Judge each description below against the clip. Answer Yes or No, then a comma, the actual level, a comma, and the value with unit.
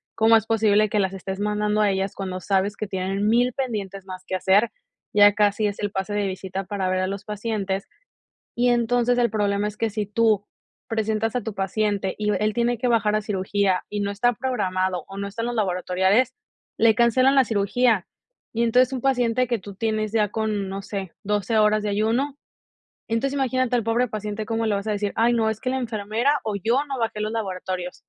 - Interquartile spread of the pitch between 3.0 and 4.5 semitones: No, narrow, 2.6 semitones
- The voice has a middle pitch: No, high, 210 Hz